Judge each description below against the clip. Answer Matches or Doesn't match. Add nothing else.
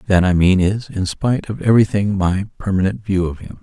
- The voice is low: Matches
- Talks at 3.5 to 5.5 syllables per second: Doesn't match